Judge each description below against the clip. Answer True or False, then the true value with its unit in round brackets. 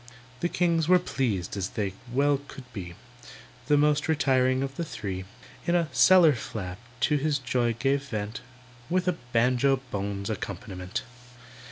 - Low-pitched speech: True (130 Hz)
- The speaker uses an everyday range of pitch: False (6.2 semitones)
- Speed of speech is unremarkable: True (150 wpm)